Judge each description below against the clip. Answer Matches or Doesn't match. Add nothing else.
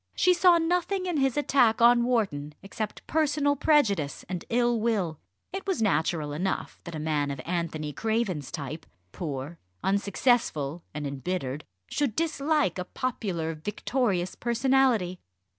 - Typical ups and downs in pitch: Doesn't match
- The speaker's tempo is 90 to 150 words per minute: Matches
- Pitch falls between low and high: Doesn't match